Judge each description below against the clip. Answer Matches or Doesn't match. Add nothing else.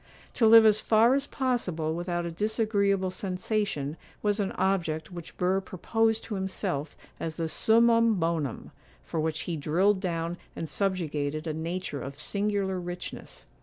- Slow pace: Doesn't match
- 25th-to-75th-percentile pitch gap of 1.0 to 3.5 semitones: Doesn't match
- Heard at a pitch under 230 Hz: Matches